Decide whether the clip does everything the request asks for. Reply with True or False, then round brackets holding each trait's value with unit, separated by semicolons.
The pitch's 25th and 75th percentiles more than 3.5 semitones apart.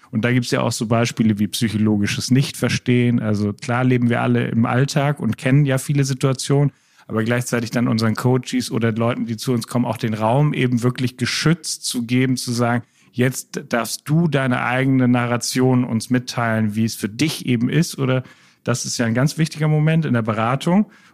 False (2.5 semitones)